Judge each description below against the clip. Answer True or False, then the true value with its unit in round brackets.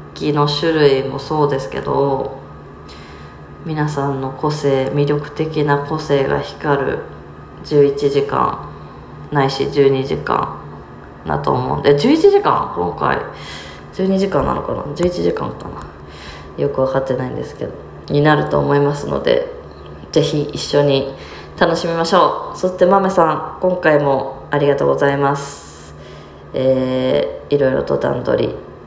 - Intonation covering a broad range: False (2.7 semitones)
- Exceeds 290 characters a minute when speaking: False (245 characters per minute)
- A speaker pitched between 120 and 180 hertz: True (140 Hz)